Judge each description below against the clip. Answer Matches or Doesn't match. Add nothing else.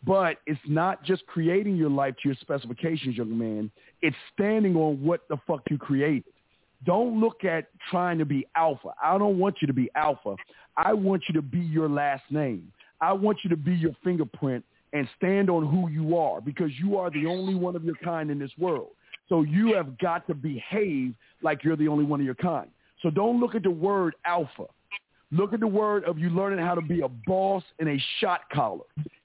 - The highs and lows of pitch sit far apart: Doesn't match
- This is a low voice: Doesn't match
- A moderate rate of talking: Doesn't match